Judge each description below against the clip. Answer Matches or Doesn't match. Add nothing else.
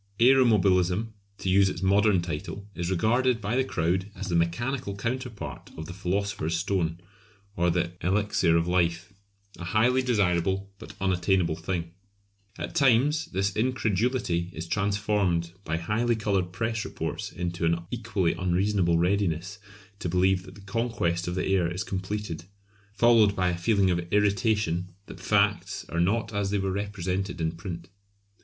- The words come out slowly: Doesn't match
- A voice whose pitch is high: Doesn't match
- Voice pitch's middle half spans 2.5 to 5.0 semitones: Matches